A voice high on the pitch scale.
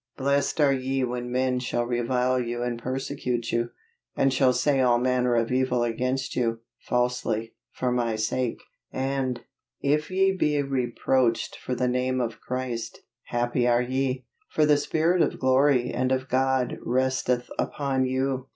No: low, 130 Hz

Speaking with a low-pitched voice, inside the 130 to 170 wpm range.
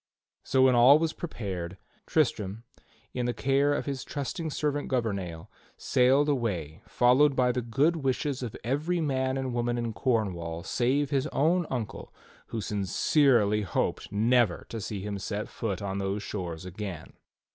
Yes: low, 120 Hz; average, 160 wpm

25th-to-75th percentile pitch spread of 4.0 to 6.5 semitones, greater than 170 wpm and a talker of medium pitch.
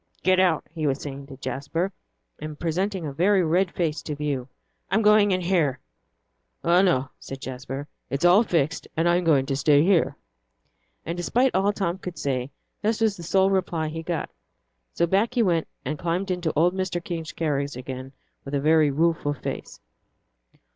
Yes: average, 4.4 semitones; average, 180 wpm; medium, 165 Hz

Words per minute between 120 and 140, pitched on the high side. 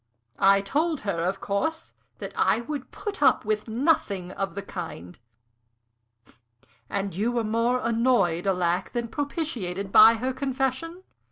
Yes: slow, 135 wpm; high, 225 Hz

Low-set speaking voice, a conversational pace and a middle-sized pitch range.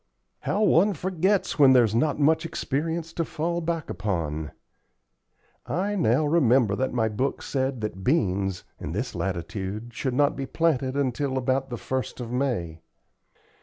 No: low, 130 Hz; average, 150 wpm; wide, 6.3 semitones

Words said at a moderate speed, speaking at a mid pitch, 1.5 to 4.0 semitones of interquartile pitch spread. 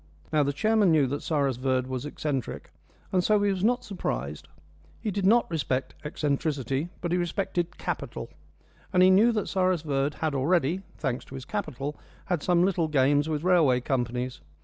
No: average, 175 wpm; medium, 155 Hz; wide, 5.4 semitones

